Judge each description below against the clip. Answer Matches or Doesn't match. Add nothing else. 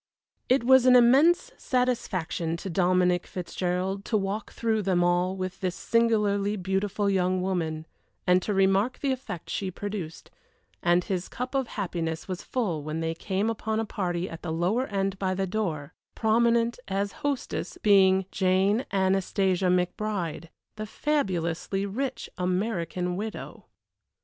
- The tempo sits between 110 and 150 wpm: Matches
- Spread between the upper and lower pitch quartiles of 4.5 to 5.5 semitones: Doesn't match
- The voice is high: Matches